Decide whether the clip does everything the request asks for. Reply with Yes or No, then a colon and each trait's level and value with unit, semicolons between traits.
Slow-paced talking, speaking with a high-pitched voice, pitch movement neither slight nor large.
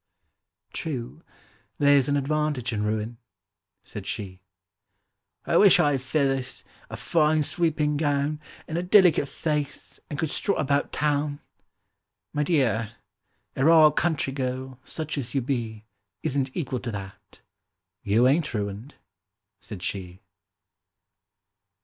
No: slow, 125 wpm; medium, 140 Hz; average, 4.5 semitones